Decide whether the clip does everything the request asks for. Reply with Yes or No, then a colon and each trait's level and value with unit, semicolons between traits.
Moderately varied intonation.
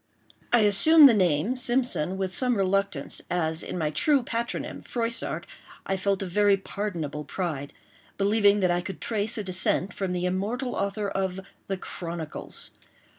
Yes: average, 3.5 semitones